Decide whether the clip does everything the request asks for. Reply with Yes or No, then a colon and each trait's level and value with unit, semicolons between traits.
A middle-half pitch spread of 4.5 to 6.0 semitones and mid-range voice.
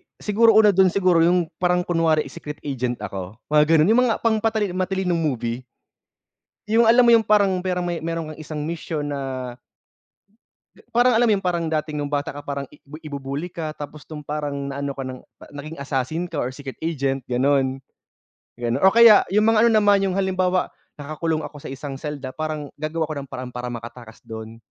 Yes: average, 5.1 semitones; medium, 155 Hz